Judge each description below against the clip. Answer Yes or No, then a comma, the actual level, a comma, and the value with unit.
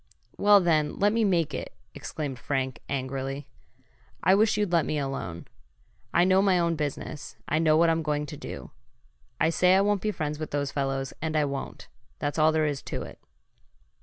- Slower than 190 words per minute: No, average, 195 wpm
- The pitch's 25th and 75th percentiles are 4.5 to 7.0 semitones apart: No, average, 3.8 semitones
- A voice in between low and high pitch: Yes, medium, 155 Hz